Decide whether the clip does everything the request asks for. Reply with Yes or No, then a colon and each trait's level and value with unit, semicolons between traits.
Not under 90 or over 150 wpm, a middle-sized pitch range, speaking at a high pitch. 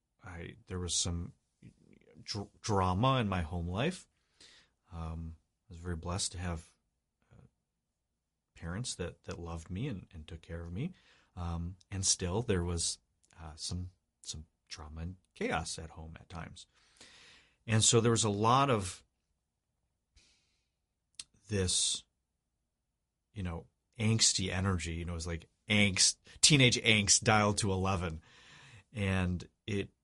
No: average, 140 wpm; average, 4.0 semitones; very low, 90 Hz